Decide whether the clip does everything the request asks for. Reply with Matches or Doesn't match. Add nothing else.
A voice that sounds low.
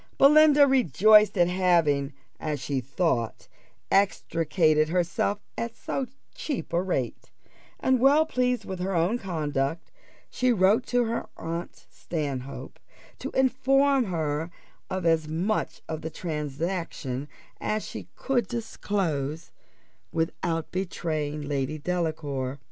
Doesn't match